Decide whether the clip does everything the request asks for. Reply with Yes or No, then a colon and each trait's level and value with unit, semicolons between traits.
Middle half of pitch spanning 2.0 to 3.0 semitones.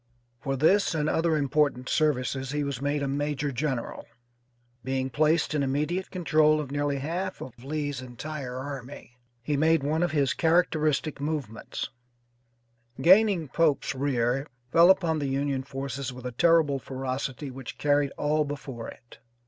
Yes: narrow, 2.6 semitones